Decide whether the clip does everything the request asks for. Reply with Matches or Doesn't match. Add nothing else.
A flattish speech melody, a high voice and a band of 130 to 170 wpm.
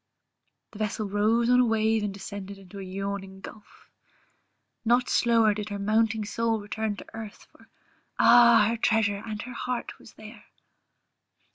Matches